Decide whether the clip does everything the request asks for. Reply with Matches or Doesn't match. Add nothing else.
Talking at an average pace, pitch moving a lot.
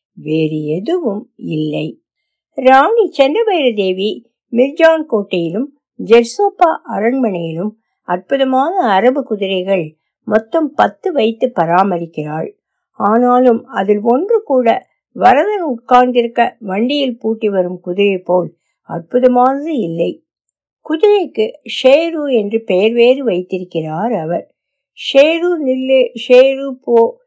Matches